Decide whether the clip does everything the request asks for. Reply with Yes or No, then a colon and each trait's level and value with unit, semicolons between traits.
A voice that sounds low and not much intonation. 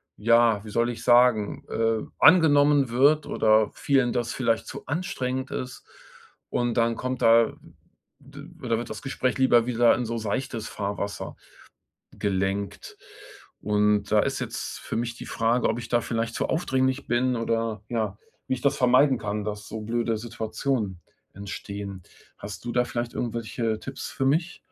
No: low, 115 Hz; average, 3.0 semitones